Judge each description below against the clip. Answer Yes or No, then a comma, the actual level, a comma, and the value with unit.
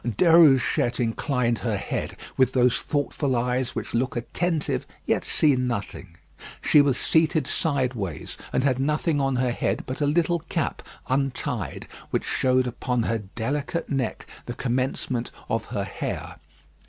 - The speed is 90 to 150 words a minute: Yes, average, 140 wpm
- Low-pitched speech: Yes, low, 130 Hz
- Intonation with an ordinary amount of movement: Yes, average, 3.1 semitones